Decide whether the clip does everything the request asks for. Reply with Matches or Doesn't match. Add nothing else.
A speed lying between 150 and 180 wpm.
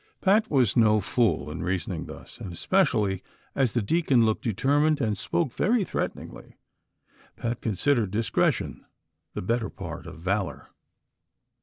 Doesn't match